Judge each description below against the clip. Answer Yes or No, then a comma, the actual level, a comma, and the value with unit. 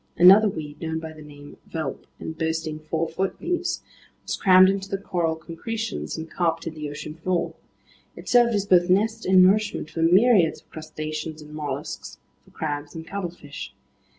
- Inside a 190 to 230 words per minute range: No, average, 170 wpm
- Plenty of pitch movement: No, average, 3.7 semitones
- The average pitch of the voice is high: No, medium, 165 Hz